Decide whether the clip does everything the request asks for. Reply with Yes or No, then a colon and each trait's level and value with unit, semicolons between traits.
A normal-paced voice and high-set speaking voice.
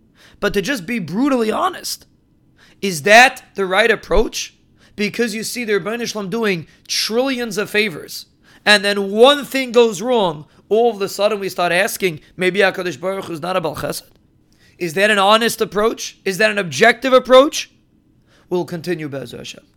Yes: average, 165 wpm; high, 210 Hz